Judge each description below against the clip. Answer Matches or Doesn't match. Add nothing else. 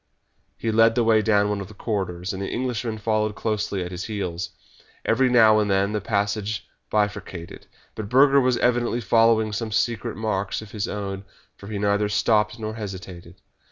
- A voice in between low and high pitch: Doesn't match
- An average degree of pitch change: Doesn't match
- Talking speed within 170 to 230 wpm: Matches